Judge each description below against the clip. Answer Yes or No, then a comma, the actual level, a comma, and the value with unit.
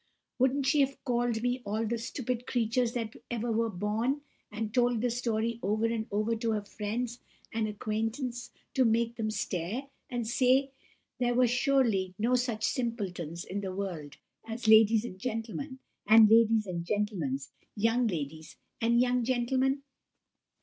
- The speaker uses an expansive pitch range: No, narrow, 2.6 semitones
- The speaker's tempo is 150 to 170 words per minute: Yes, average, 155 wpm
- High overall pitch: Yes, high, 230 Hz